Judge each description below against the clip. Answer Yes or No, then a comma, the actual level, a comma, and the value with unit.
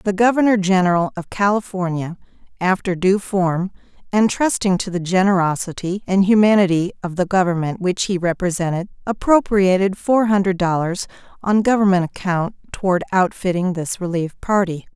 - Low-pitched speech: No, high, 190 Hz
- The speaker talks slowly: Yes, slow, 130 wpm